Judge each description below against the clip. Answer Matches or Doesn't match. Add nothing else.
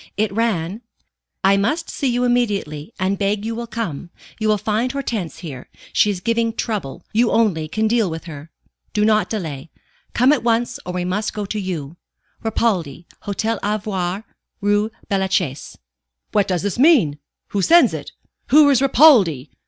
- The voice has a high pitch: Matches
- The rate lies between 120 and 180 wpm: Matches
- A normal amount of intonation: Matches